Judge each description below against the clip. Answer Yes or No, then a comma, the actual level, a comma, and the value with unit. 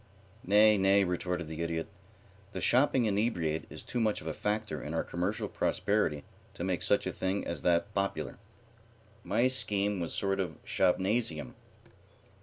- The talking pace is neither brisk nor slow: Yes, average, 160 wpm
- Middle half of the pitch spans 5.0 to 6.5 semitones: No, average, 4.1 semitones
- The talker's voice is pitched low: Yes, very low, 95 Hz